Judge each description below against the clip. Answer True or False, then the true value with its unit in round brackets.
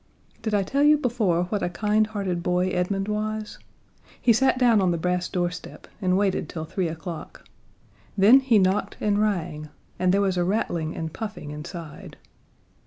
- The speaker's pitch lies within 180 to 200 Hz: True (190 Hz)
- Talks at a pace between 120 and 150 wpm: False (170 wpm)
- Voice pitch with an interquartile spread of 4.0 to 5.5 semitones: False (3.4 semitones)